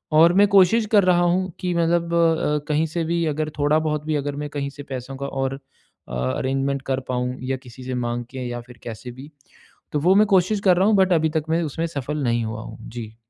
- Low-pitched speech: No, medium, 150 Hz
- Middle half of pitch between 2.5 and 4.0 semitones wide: No, average, 4.9 semitones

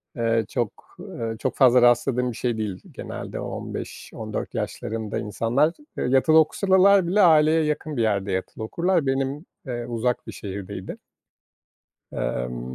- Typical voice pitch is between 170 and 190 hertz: No, low, 125 Hz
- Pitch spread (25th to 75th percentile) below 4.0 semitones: No, wide, 5.6 semitones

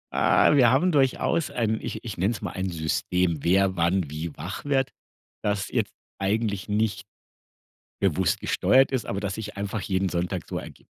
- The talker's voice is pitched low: Yes, low, 100 Hz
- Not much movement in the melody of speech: No, average, 3.8 semitones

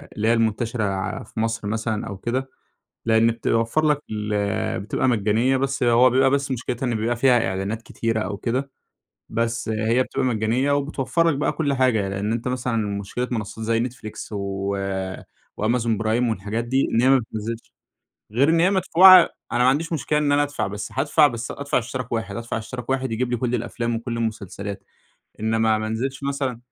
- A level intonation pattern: No, average, 3.2 semitones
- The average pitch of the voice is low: Yes, low, 115 Hz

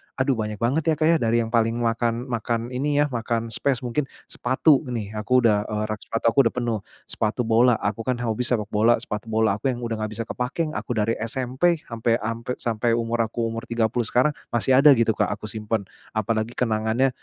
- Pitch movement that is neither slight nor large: No, narrow, 2.1 semitones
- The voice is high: No, low, 115 Hz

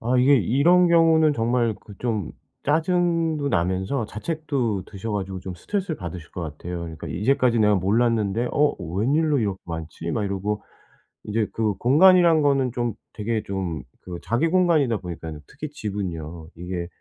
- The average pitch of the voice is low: Yes, low, 115 Hz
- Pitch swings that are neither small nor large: No, wide, 7.5 semitones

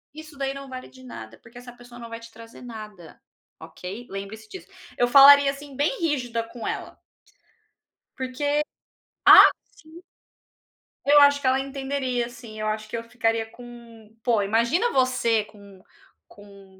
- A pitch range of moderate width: Yes, average, 3.8 semitones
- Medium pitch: No, high, 240 Hz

